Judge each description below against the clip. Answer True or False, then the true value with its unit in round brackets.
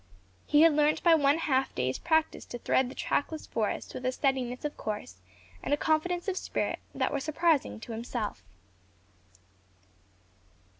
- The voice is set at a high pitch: True (285 Hz)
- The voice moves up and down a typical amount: True (4.3 semitones)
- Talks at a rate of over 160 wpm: False (155 wpm)